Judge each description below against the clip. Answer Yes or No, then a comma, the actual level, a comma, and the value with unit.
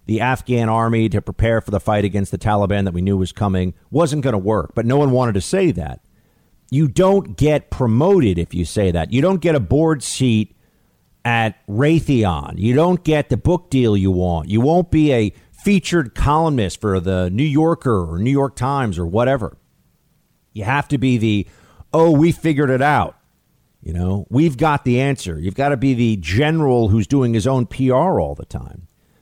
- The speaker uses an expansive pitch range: Yes, wide, 6.1 semitones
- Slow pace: No, average, 200 wpm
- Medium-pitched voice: No, low, 120 Hz